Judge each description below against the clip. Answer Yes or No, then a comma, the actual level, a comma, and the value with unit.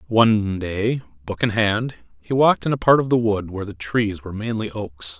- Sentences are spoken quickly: Yes, fast, 220 wpm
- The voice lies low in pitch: Yes, low, 105 Hz